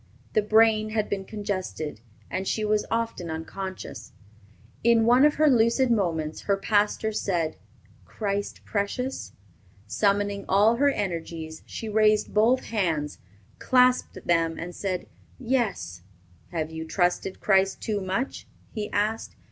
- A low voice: No, high, 205 Hz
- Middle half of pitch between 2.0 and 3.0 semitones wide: No, average, 3.9 semitones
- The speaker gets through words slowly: Yes, slow, 130 wpm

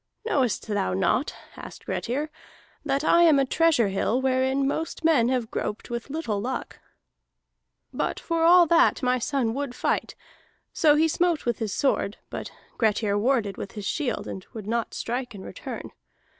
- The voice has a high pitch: Yes, very high, 255 Hz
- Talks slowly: No, average, 165 wpm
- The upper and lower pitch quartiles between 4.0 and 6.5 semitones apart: Yes, average, 5.2 semitones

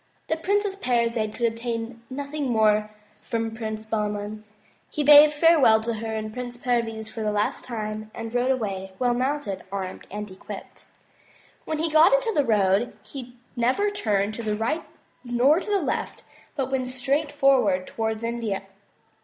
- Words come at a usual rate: Yes, average, 160 wpm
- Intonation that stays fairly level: No, average, 4.1 semitones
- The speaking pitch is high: Yes, high, 235 Hz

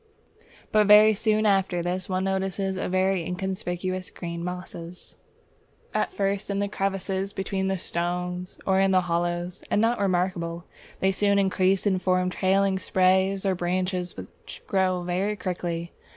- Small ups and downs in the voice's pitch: Yes, narrow, 1.4 semitones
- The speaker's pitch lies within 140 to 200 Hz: Yes, medium, 185 Hz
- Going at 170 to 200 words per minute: No, average, 140 wpm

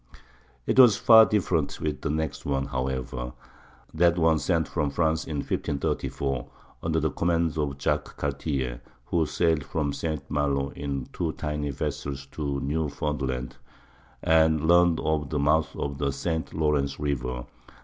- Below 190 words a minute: Yes, average, 140 wpm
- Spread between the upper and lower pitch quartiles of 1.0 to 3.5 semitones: Yes, narrow, 2.6 semitones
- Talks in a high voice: No, very low, 75 Hz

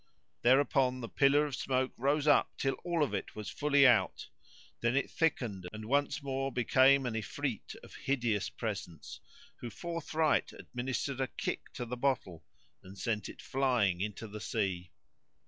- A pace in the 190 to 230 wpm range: No, average, 160 wpm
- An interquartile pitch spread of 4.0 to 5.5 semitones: Yes, average, 4.4 semitones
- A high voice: No, low, 130 Hz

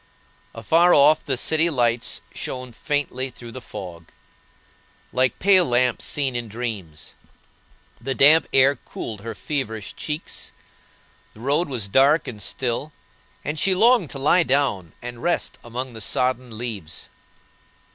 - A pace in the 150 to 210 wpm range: No, slow, 135 wpm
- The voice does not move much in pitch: No, average, 4.2 semitones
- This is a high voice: No, low, 130 Hz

